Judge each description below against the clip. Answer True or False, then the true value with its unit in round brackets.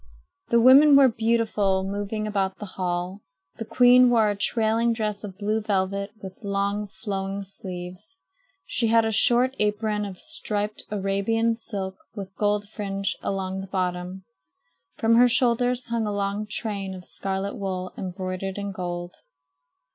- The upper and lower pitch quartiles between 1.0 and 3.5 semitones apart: True (2.7 semitones)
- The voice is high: True (205 Hz)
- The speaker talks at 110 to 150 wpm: True (145 wpm)